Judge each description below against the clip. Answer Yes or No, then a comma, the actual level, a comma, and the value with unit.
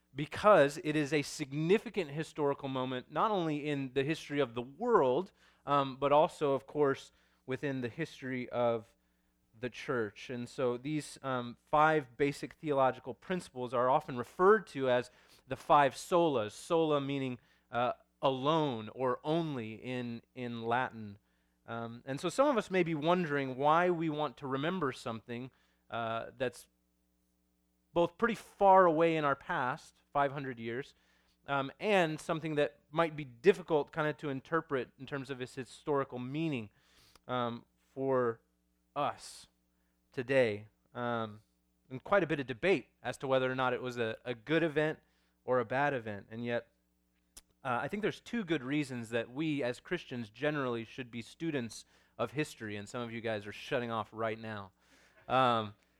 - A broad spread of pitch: No, average, 4.8 semitones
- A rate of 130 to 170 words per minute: Yes, average, 160 wpm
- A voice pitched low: Yes, low, 130 Hz